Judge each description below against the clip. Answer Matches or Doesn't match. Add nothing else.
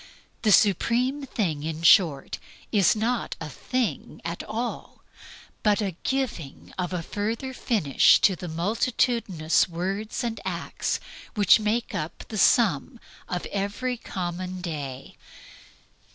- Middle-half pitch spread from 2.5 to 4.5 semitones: Doesn't match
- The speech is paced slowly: Matches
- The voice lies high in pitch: Matches